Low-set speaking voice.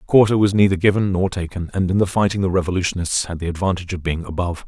Yes: very low, 90 Hz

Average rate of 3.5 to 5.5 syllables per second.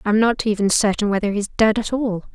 No: 6.4 syllables/s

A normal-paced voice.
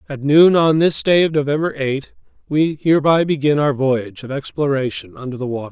Yes: average, 190 wpm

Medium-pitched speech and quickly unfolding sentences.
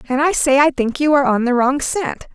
No: very high, 275 Hz; fast, 280 wpm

